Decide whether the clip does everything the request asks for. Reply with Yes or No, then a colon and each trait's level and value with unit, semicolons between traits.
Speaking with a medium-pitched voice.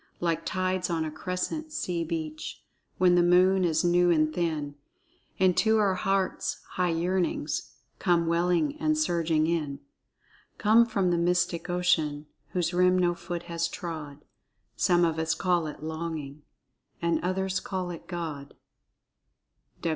Yes: medium, 175 Hz